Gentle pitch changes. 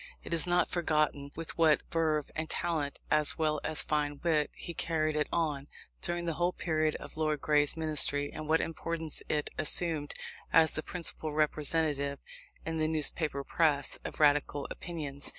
Yes: narrow, 1.7 semitones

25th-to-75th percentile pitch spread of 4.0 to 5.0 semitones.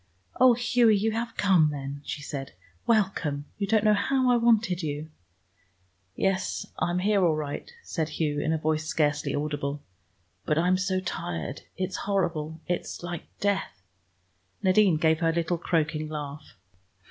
Yes: average, 4.7 semitones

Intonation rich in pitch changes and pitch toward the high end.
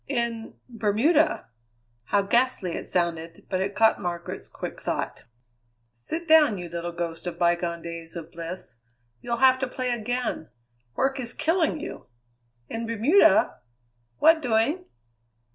Yes: wide, 7.0 semitones; high, 220 Hz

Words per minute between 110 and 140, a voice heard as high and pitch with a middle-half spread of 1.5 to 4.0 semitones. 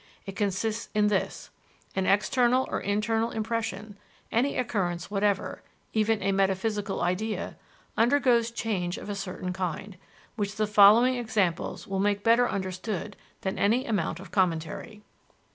Yes: slow, 135 wpm; high, 205 Hz; average, 2.8 semitones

